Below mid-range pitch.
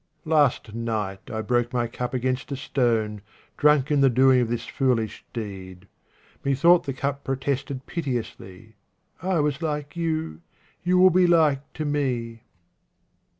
Yes: low, 130 Hz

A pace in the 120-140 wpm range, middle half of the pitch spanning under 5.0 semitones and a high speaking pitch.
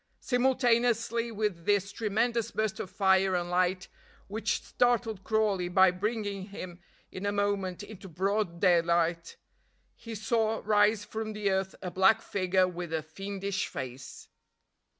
Yes: slow, 135 wpm; average, 3.0 semitones; high, 200 Hz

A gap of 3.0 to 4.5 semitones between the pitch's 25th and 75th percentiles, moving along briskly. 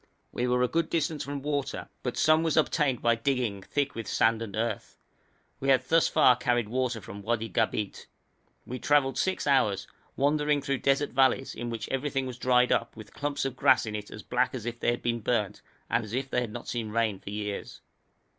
Yes: average, 3.5 semitones; fast, 210 wpm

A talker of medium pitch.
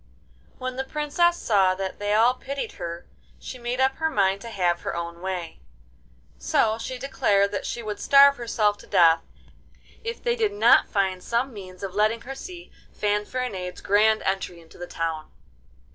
No: high, 210 Hz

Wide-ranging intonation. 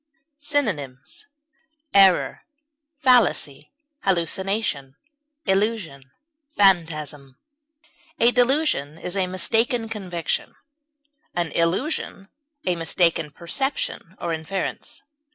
Yes: wide, 6.0 semitones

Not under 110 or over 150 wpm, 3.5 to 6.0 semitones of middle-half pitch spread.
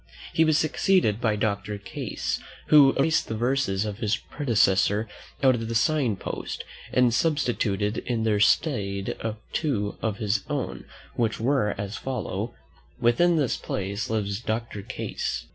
Yes: average, 145 wpm; average, 4.5 semitones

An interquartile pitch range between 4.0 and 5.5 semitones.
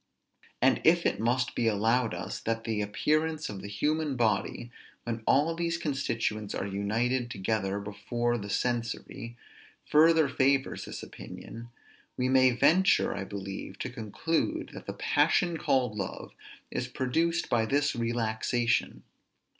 Yes: average, 4.9 semitones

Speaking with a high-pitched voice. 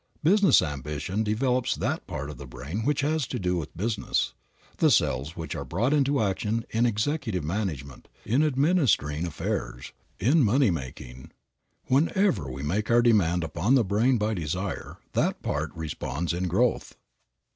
No: low, 100 Hz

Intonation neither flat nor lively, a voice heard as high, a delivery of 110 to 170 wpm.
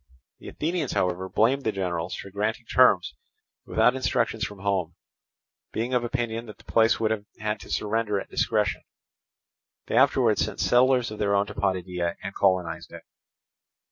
No: average, 3.8 semitones; low, 105 Hz; average, 165 wpm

